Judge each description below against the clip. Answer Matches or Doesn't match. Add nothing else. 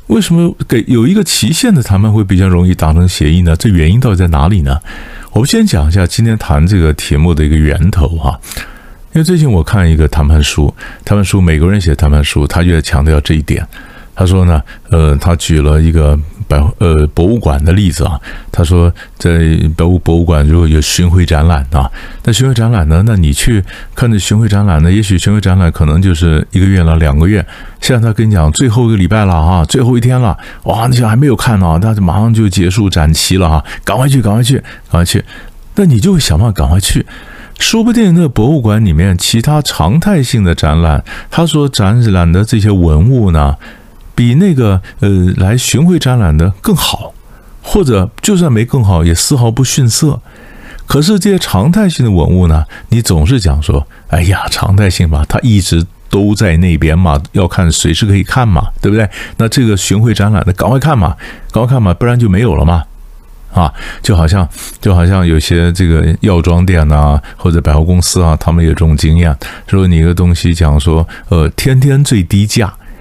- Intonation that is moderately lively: Doesn't match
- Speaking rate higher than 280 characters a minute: Matches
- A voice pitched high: Doesn't match